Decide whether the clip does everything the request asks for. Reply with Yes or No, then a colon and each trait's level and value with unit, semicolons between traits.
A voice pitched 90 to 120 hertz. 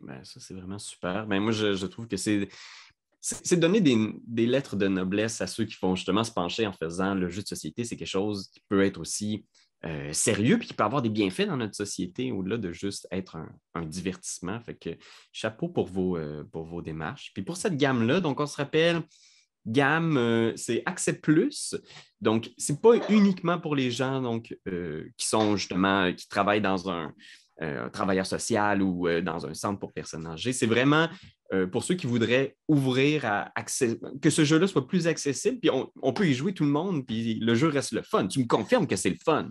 Yes: low, 110 Hz